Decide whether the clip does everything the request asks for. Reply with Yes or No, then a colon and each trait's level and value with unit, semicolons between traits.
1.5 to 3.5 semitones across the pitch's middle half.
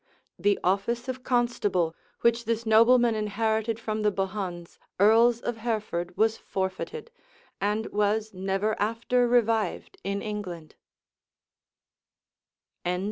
Yes: average, 2.8 semitones